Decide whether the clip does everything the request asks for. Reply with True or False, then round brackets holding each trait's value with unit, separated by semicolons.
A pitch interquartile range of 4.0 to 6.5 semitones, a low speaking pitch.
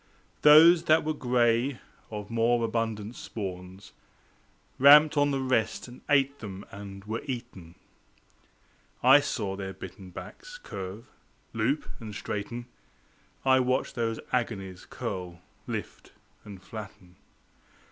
True (5.1 semitones; 115 Hz)